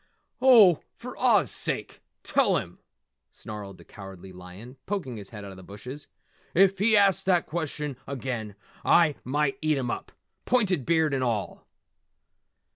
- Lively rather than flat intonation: Yes, wide, 8.7 semitones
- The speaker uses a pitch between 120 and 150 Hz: Yes, low, 135 Hz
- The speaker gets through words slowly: No, average, 150 wpm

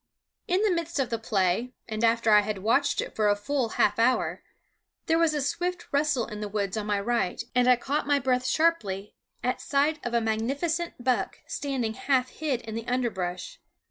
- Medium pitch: No, very high, 250 Hz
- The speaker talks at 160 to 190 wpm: No, average, 200 wpm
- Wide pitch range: No, average, 4.9 semitones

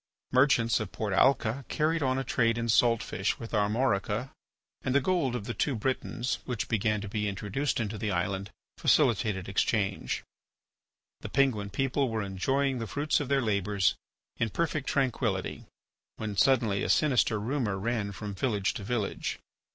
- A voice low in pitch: Yes, low, 115 Hz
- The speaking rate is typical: Yes, average, 160 wpm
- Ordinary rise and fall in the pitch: Yes, average, 4.5 semitones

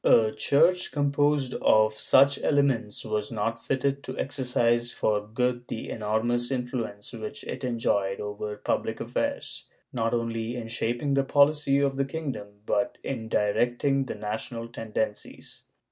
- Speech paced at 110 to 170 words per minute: Yes, average, 145 wpm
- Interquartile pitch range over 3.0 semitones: Yes, average, 3.9 semitones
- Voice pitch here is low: Yes, low, 120 Hz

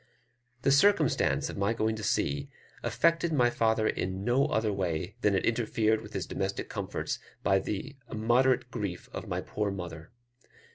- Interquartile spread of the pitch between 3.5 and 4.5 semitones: Yes, average, 4.0 semitones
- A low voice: Yes, low, 110 Hz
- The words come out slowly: No, average, 160 wpm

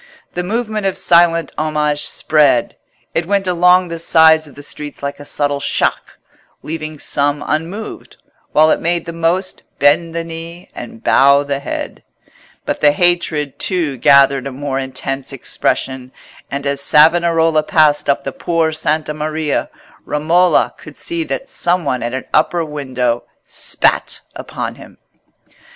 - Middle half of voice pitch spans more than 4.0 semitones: No, average, 3.1 semitones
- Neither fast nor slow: Yes, average, 150 wpm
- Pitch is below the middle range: No, medium, 155 Hz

